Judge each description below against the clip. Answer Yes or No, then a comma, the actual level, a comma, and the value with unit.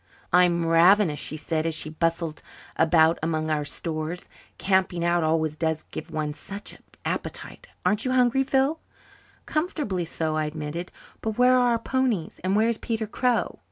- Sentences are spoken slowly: No, average, 165 wpm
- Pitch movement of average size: No, wide, 6.0 semitones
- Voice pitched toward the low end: No, medium, 175 Hz